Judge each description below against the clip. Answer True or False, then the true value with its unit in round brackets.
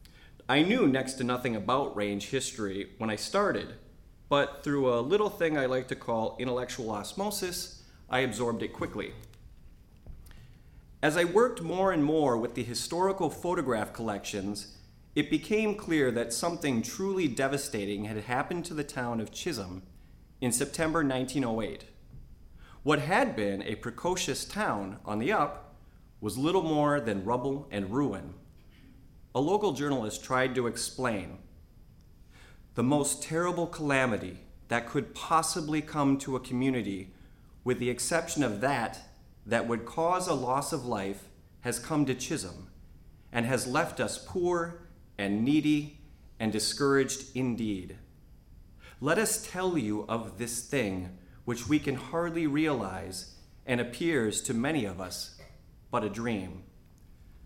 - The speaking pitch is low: True (125 Hz)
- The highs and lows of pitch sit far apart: True (6.2 semitones)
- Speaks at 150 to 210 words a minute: False (140 wpm)